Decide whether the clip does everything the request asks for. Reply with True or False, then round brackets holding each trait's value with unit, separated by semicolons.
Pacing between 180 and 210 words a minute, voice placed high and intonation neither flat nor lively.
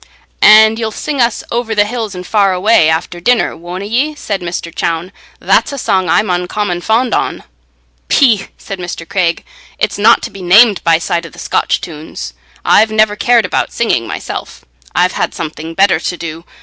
True (185 wpm; 195 Hz; 4.3 semitones)